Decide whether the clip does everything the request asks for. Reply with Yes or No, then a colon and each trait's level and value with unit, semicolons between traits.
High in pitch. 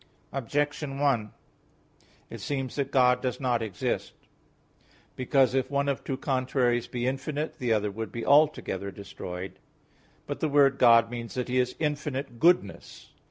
No: low, 130 Hz